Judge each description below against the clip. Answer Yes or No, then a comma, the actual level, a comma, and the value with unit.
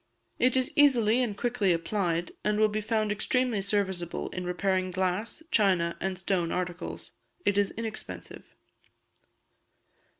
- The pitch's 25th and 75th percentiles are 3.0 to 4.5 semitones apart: Yes, average, 3.3 semitones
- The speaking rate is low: Yes, slow, 130 wpm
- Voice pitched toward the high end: Yes, high, 200 Hz